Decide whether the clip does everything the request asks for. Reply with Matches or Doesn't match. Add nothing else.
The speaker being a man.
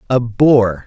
Matches